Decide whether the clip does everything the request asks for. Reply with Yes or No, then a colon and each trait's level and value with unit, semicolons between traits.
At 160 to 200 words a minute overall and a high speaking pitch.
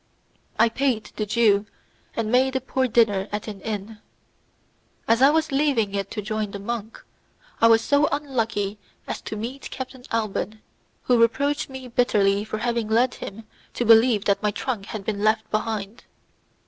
Yes: average, 170 wpm; high, 225 Hz